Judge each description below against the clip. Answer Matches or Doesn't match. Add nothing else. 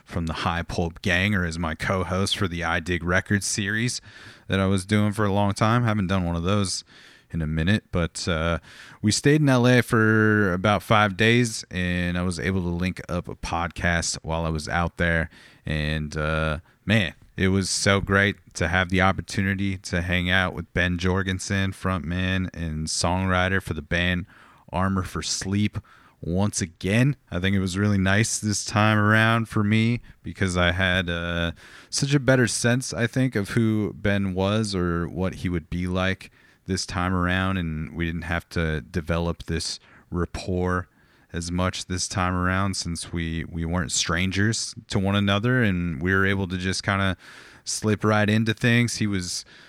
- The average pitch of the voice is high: Doesn't match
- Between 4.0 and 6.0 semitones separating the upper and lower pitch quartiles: Doesn't match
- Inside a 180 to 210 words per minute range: Matches